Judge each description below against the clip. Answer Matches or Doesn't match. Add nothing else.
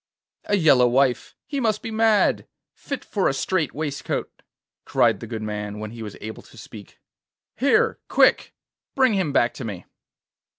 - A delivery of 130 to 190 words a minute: Matches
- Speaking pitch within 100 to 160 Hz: Matches